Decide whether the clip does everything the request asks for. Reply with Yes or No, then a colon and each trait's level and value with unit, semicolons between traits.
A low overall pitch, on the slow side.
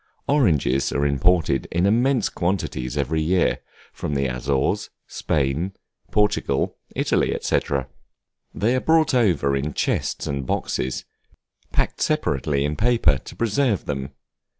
Yes: very low, 80 Hz; slow, 125 wpm